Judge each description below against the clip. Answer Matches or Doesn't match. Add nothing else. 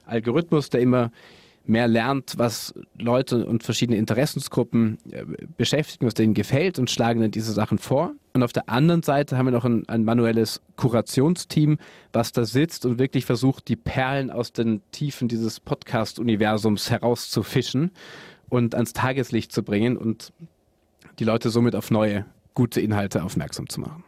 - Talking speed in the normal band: Matches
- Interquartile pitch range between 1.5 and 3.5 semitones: Matches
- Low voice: Matches